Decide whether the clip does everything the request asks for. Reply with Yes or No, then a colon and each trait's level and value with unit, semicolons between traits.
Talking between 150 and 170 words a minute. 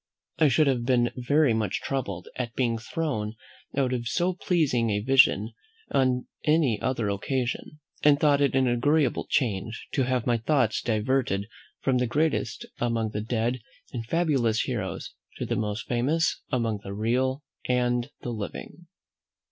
Yes: average, 155 wpm